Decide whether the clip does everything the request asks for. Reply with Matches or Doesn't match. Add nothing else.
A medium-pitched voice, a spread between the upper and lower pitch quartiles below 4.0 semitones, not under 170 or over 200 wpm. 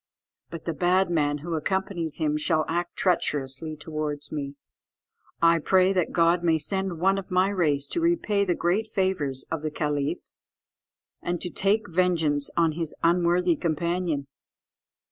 Doesn't match